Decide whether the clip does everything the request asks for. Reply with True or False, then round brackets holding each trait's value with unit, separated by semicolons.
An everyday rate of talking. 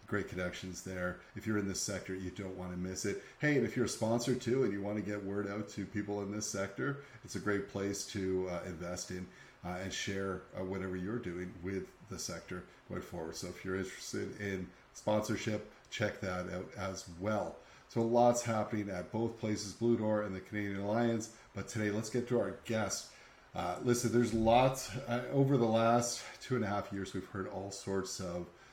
False (210 wpm)